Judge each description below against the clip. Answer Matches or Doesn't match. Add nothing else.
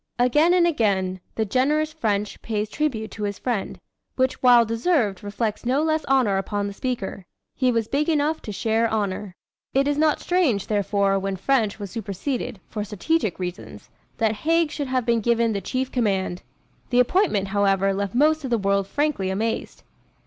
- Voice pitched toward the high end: Matches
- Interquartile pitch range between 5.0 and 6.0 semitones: Matches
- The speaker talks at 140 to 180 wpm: Matches